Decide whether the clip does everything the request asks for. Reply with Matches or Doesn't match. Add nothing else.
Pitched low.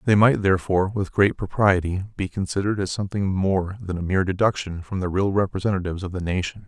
Matches